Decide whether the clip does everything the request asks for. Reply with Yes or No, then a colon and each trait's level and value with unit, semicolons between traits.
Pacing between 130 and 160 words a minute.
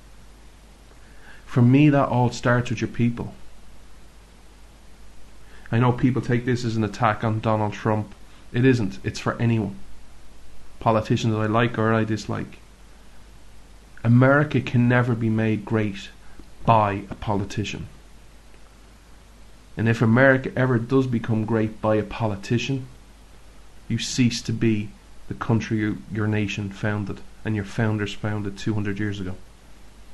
Yes: slow, 135 wpm